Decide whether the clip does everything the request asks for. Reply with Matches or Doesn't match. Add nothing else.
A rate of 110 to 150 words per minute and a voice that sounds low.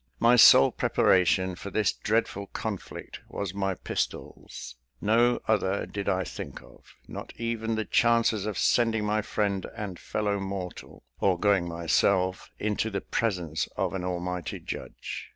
Matches